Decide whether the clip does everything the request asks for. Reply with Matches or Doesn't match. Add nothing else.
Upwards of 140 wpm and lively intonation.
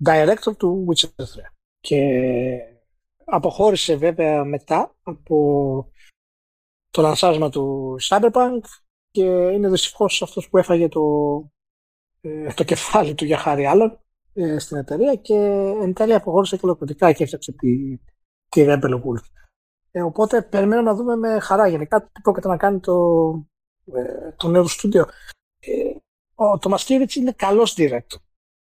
Doesn't match